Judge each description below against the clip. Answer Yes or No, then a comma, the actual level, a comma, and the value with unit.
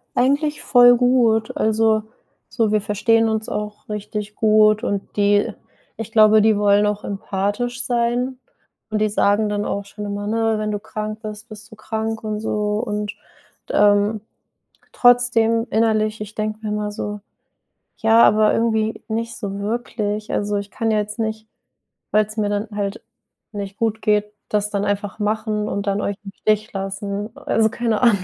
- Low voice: No, high, 215 Hz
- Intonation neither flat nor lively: No, narrow, 1.3 semitones